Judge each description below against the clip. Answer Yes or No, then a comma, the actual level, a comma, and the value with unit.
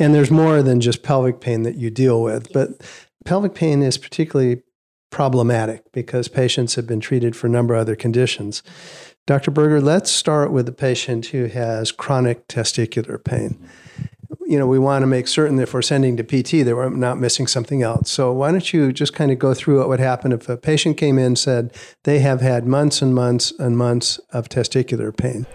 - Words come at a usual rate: No, fast, 210 wpm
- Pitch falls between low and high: No, low, 130 Hz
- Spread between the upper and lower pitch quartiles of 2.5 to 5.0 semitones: Yes, average, 2.8 semitones